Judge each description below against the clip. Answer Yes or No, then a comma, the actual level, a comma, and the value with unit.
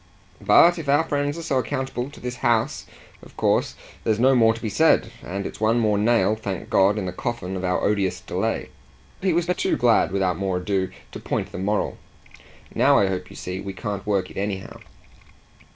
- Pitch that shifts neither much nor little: Yes, average, 4.5 semitones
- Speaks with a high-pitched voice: No, low, 105 Hz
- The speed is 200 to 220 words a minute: Yes, fast, 205 wpm